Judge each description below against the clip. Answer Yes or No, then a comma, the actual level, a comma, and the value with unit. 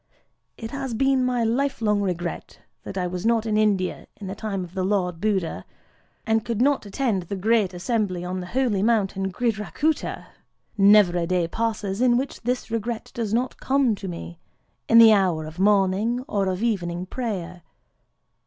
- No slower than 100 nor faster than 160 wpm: No, average, 175 wpm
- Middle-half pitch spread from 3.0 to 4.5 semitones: Yes, average, 4.0 semitones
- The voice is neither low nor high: No, high, 210 Hz